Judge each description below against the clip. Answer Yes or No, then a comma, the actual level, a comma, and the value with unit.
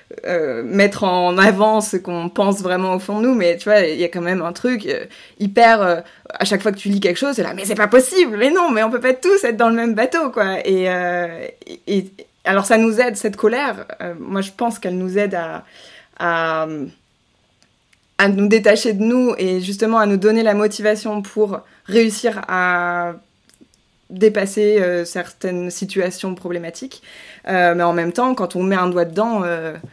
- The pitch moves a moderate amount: Yes, average, 3.8 semitones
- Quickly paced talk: No, average, 205 wpm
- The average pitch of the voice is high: Yes, high, 200 Hz